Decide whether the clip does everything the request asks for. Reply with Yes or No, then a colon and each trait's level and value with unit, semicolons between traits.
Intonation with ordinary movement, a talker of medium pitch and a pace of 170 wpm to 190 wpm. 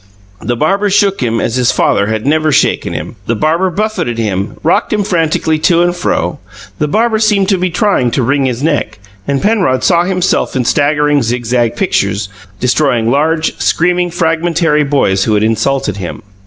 No: wide, 6.9 semitones; medium, 150 Hz; average, 175 wpm